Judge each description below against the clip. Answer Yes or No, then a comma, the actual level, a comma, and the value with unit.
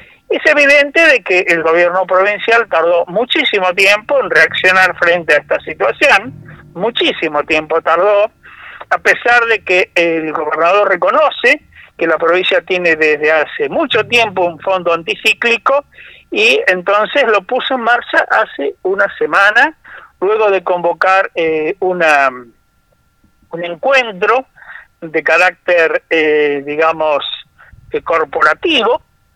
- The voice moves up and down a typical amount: No, wide, 6.4 semitones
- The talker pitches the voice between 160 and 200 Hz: Yes, medium, 185 Hz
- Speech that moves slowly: Yes, slow, 120 wpm